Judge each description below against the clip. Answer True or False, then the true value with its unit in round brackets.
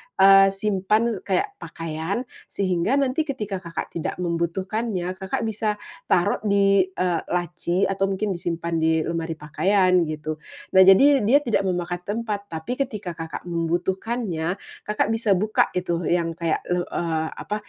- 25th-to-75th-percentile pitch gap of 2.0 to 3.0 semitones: False (3.7 semitones)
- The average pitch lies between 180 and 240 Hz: True (190 Hz)